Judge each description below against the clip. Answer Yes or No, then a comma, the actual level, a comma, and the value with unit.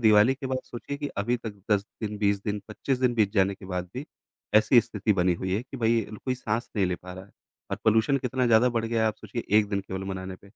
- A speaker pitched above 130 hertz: No, low, 110 Hz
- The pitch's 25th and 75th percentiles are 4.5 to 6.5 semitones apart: No, average, 3.5 semitones